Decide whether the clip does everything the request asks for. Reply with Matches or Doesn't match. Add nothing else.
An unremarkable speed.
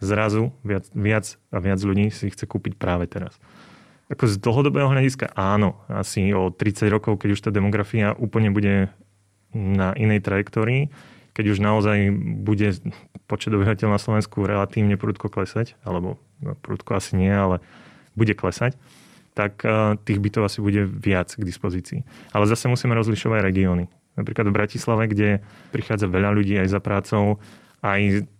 Matches